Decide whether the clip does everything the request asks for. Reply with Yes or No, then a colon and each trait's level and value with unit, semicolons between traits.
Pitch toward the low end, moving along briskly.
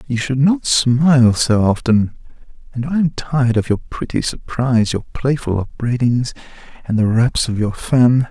No: low, 125 Hz; average, 165 wpm